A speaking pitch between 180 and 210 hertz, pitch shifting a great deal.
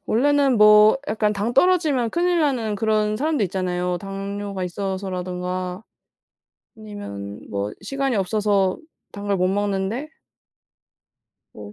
No: high, 205 Hz; average, 3.7 semitones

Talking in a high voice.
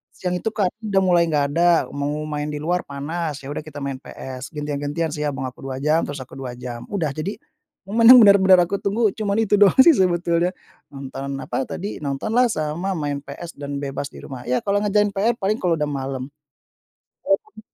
No: medium, 155 Hz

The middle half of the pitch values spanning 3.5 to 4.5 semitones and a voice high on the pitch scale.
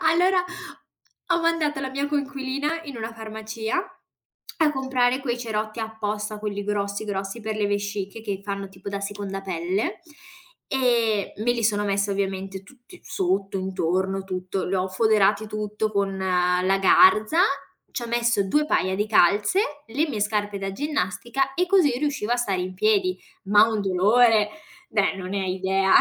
Yes: average, 3.9 semitones; high, 210 Hz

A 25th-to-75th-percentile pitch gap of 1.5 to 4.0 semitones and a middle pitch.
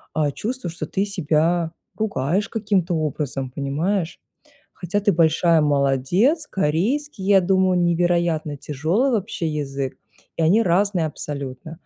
No: average, 4.8 semitones; medium, 170 Hz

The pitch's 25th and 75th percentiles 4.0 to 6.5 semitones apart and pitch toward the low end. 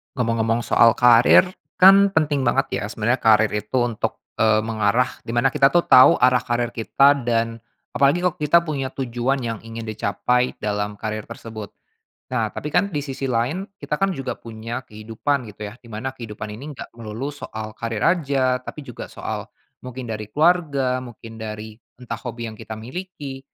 No: average, 3.6 semitones; low, 120 Hz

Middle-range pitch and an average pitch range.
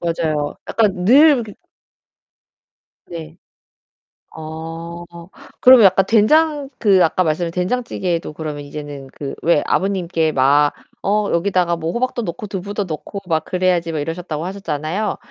Yes: medium, 175 Hz; average, 4.2 semitones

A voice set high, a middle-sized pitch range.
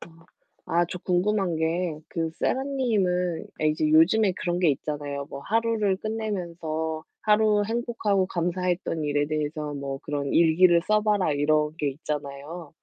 No: medium, 170 Hz; average, 4.7 semitones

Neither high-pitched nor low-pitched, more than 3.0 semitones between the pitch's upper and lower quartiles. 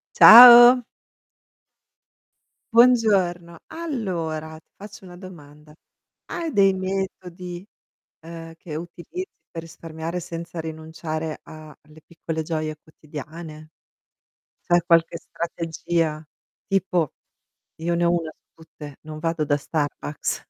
No: medium, 165 Hz; average, 2.7 semitones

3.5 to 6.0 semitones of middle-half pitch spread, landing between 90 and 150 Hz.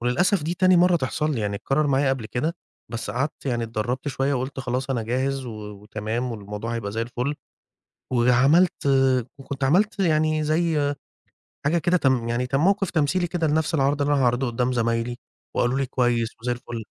Yes: average, 4.3 semitones; low, 135 Hz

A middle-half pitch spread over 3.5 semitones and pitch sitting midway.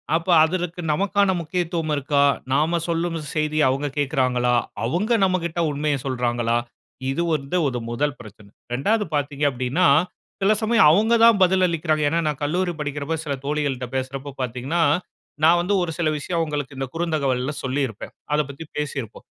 Yes: average, 4.1 semitones; medium, 150 Hz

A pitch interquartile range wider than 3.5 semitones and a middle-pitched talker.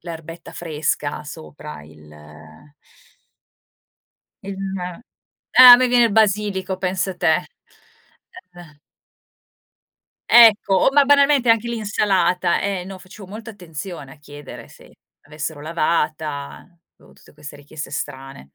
Yes: average, 5.3 semitones; medium, 180 Hz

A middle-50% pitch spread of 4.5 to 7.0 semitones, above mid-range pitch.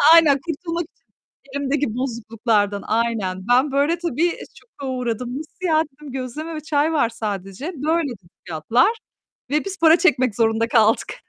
Yes: wide, 5.5 semitones; very high, 265 Hz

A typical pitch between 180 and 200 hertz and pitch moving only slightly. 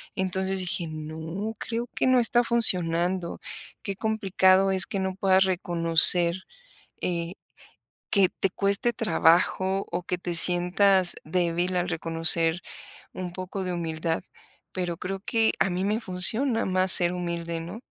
Yes: medium, 185 Hz; narrow, 2.2 semitones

